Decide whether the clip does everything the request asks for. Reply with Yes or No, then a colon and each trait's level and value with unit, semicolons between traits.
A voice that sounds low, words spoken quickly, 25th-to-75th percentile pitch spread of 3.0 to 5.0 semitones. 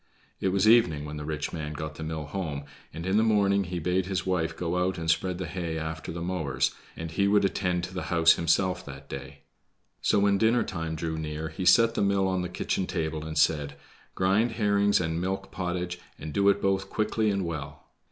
Yes: very low, 90 Hz; fast, 220 wpm; average, 3.6 semitones